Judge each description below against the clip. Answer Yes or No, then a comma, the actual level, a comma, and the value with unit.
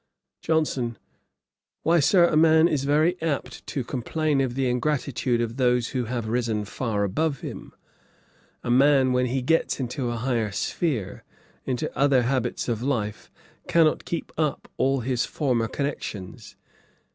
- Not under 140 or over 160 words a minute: Yes, average, 145 wpm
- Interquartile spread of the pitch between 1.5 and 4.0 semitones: Yes, average, 3.7 semitones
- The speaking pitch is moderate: No, low, 130 Hz